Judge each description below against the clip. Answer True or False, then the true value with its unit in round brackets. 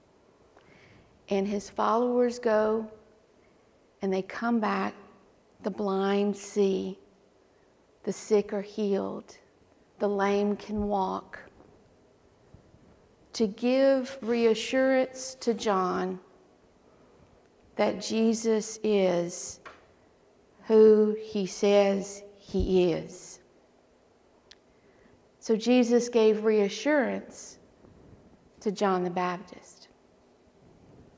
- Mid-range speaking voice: False (210 Hz)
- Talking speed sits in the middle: False (75 wpm)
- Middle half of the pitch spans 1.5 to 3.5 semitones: True (2.4 semitones)